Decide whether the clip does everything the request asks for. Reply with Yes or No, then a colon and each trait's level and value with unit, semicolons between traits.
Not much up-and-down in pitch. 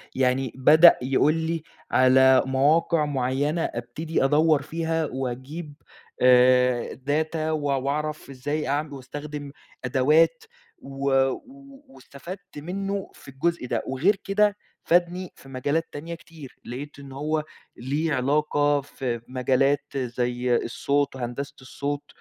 No: average, 3.5 semitones